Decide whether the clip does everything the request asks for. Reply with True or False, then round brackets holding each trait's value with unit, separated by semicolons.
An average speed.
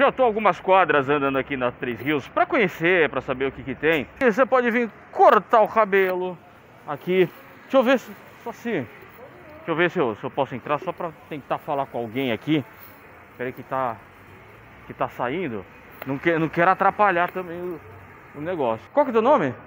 False (205 wpm)